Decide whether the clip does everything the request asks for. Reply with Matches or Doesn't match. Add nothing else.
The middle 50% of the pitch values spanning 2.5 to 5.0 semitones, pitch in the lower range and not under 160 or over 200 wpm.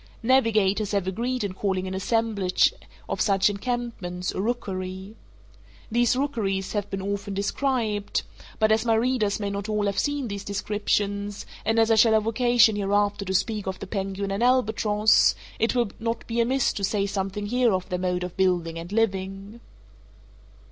Doesn't match